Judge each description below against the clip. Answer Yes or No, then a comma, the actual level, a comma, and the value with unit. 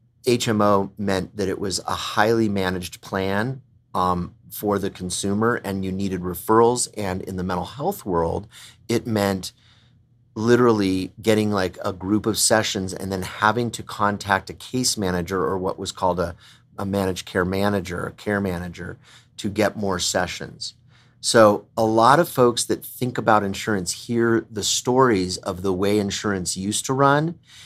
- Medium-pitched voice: No, low, 100 Hz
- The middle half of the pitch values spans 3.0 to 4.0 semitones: Yes, average, 3.4 semitones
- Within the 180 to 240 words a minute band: No, average, 165 wpm